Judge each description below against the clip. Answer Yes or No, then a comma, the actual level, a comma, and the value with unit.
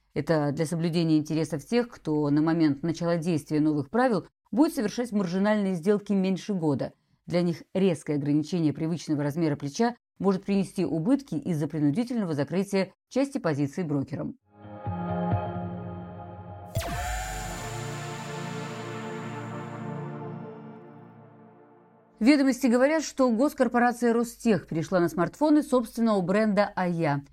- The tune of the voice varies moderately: No, wide, 6.9 semitones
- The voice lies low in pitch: No, medium, 170 Hz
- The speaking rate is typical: No, slow, 100 wpm